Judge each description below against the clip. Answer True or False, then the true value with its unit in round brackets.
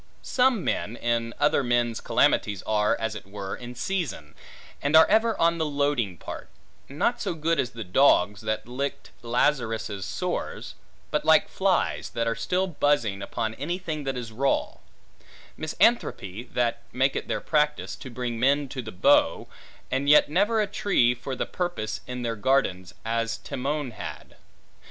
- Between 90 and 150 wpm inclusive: False (165 wpm)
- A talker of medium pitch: False (125 Hz)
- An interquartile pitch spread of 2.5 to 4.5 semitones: False (4.9 semitones)